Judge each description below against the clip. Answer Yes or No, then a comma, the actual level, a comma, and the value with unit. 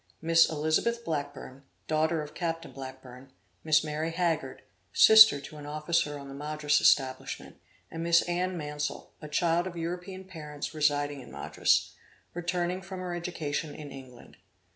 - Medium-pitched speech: Yes, medium, 155 Hz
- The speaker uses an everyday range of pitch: Yes, average, 3.0 semitones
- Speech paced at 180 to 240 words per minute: No, average, 145 wpm